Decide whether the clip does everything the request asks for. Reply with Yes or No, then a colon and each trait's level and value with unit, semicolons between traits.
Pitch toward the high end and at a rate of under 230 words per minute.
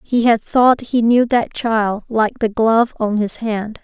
Yes: high, 225 Hz; fast, 205 wpm